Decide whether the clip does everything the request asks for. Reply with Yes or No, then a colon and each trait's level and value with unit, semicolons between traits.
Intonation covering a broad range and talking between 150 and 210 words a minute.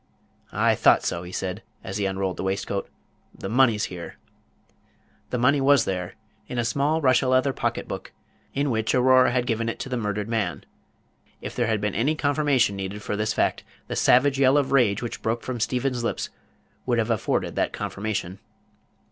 No: average, 4.2 semitones; average, 185 wpm